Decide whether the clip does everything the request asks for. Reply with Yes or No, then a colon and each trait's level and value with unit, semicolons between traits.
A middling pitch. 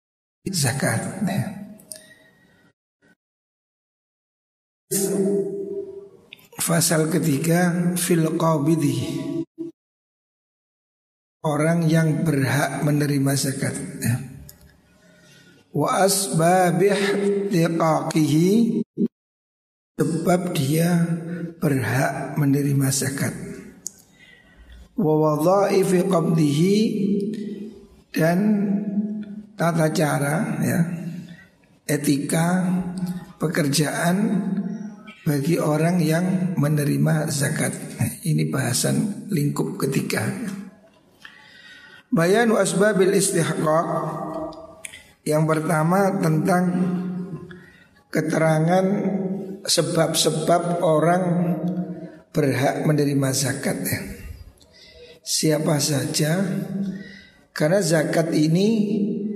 Yes: medium, 170 Hz